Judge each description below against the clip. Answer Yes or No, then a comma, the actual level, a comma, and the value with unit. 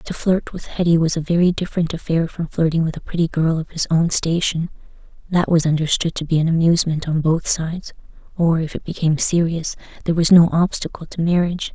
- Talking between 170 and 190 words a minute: No, fast, 205 wpm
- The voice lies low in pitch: No, medium, 165 Hz